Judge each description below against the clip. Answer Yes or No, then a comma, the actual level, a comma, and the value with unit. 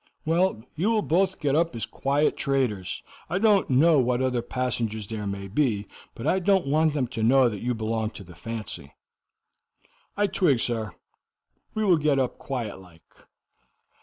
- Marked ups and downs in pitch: Yes, wide, 6.3 semitones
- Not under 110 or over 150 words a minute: No, average, 170 wpm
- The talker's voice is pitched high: No, low, 130 Hz